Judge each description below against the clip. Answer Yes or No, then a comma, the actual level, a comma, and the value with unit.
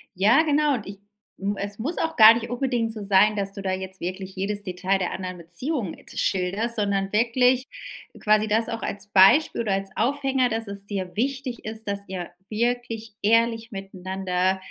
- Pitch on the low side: No, high, 210 Hz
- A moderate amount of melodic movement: Yes, average, 3.4 semitones